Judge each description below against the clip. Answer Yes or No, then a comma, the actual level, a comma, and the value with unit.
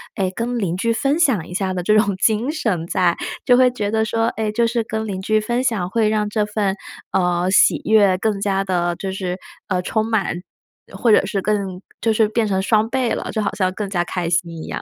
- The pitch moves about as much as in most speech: Yes, average, 3.1 semitones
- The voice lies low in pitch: No, high, 210 Hz